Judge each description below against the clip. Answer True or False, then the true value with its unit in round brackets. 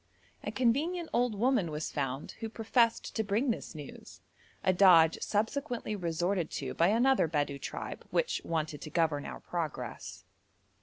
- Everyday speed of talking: True (150 wpm)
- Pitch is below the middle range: False (195 Hz)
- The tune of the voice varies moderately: False (6.8 semitones)